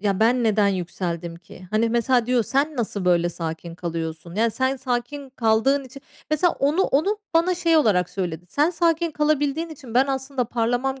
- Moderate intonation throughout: No, wide, 6.9 semitones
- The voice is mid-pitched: No, high, 245 Hz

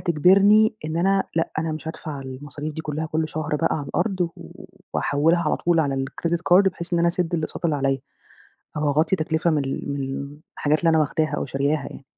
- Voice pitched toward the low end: No, medium, 155 Hz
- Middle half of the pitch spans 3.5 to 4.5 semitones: No, average, 2.8 semitones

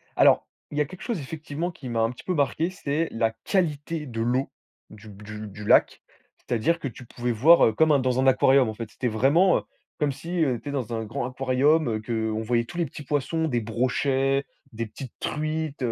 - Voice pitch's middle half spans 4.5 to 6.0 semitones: Yes, average, 4.9 semitones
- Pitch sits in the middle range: No, low, 130 Hz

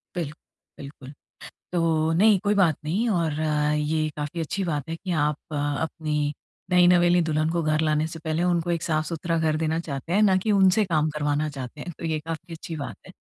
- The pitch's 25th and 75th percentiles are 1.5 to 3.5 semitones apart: Yes, narrow, 2.4 semitones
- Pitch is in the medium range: Yes, medium, 160 Hz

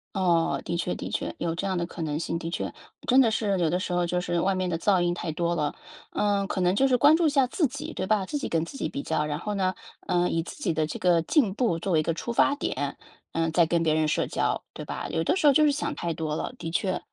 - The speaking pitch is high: No, medium, 180 Hz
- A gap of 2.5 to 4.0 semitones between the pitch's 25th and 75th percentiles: No, average, 4.4 semitones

